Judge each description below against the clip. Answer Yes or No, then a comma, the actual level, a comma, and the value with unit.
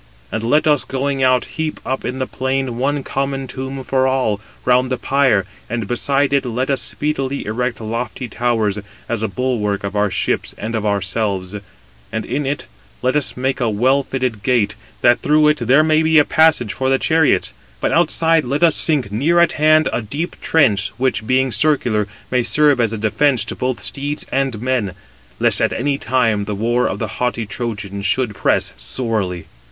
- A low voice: Yes, low, 125 Hz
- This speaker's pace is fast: No, average, 190 wpm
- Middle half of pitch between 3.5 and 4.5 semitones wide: Yes, average, 3.9 semitones